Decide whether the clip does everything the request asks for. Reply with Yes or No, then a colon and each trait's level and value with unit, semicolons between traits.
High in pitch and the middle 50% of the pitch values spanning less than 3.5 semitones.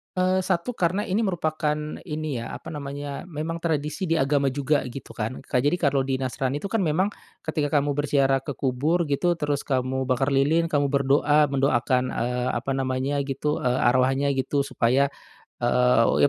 No: medium, 140 Hz; average, 2.8 semitones